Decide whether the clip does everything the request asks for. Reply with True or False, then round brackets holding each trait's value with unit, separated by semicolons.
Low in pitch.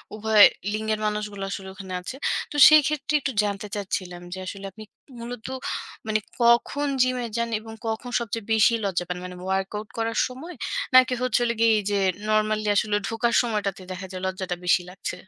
False (215 Hz)